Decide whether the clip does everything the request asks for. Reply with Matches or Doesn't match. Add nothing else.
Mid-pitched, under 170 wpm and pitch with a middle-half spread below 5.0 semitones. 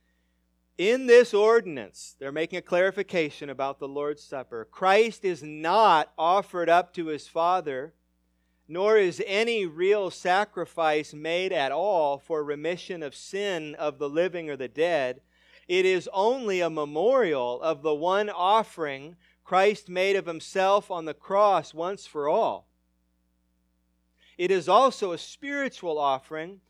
Doesn't match